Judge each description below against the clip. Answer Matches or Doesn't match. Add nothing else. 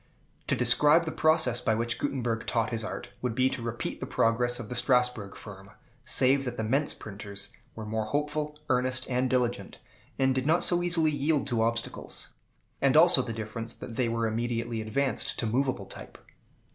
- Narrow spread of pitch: Doesn't match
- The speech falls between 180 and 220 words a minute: Matches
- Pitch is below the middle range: Matches